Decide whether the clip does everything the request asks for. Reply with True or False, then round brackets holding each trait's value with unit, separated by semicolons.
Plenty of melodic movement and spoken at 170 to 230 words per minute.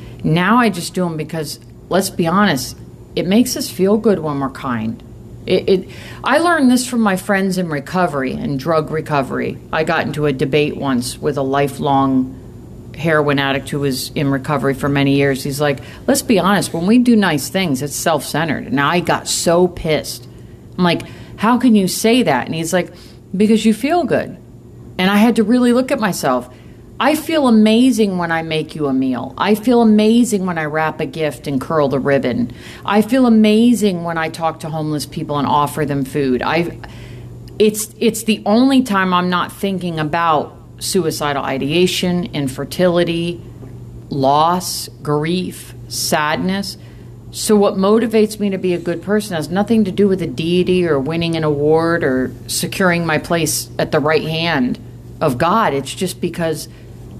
True (6.2 semitones; 180 wpm)